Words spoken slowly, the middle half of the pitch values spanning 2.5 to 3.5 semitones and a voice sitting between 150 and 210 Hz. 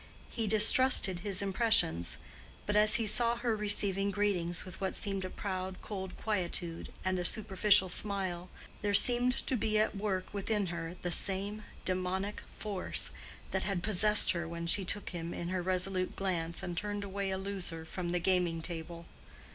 No: average, 170 wpm; average, 2.8 semitones; high, 190 Hz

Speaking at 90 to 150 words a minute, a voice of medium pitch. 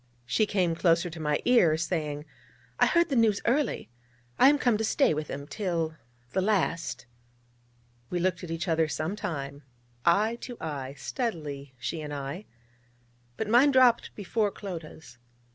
No: average, 160 wpm; medium, 170 Hz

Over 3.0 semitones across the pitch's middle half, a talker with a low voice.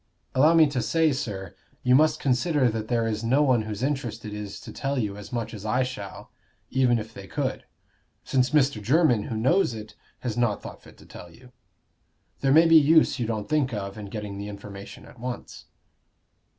Yes: average, 4.4 semitones; low, 120 Hz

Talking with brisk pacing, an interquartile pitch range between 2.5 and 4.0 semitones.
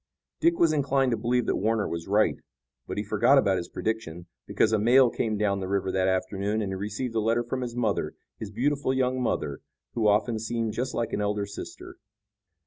Yes: fast, 210 wpm; average, 3.4 semitones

